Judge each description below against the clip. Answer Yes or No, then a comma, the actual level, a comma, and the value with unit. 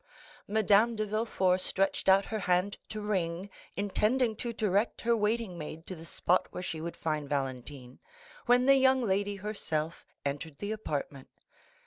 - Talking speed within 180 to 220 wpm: No, average, 155 wpm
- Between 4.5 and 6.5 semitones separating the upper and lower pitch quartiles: Yes, average, 4.8 semitones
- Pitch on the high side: Yes, high, 195 Hz